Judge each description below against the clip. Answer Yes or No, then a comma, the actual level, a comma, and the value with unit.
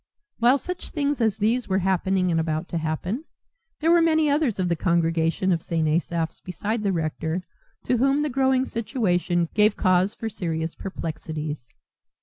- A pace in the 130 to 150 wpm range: No, average, 165 wpm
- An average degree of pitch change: No, wide, 6.8 semitones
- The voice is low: No, high, 190 Hz